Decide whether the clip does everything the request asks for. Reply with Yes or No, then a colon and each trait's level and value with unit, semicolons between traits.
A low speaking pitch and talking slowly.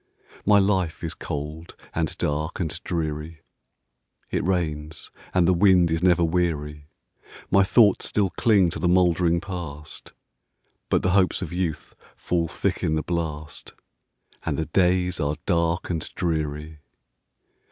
Yes: very low, 85 Hz; slow, 125 wpm